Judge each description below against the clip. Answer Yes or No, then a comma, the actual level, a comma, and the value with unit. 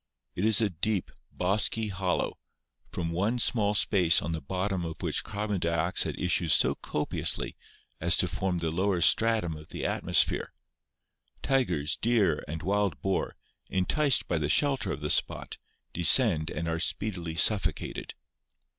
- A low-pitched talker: Yes, very low, 90 Hz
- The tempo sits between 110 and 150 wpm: Yes, average, 145 wpm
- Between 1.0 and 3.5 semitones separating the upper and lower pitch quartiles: No, average, 4.1 semitones